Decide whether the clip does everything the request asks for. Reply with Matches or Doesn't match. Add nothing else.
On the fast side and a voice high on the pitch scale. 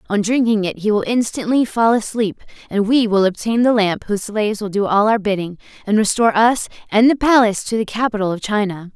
Matches